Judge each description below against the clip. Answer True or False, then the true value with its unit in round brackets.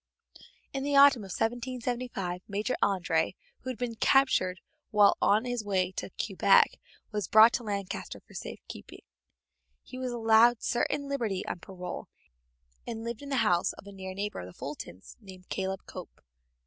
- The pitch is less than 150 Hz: False (215 Hz)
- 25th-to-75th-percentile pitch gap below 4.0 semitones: False (4.4 semitones)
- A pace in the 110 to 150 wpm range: False (165 wpm)